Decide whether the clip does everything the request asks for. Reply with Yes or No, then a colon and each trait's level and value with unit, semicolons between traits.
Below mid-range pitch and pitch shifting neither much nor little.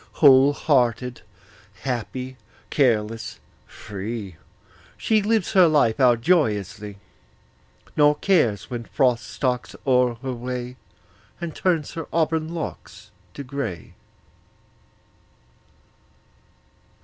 Yes: low, 125 Hz; average, 4.7 semitones